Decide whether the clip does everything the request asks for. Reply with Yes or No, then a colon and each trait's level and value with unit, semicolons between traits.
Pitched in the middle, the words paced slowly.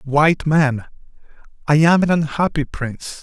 Yes: medium, 150 Hz; slow, 130 wpm